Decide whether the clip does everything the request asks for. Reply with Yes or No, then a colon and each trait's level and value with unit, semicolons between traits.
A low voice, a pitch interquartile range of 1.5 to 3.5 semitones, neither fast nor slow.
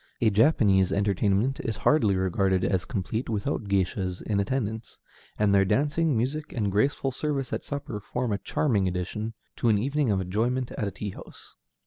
No: low, 105 Hz; average, 4.7 semitones; average, 170 wpm